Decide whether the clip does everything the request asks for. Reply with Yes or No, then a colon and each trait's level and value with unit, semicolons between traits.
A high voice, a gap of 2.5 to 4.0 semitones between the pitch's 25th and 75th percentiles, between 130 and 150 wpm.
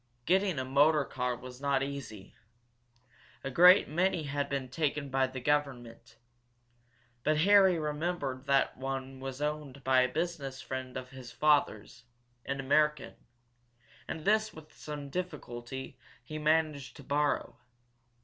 No: medium, 140 Hz; average, 2.8 semitones; slow, 135 wpm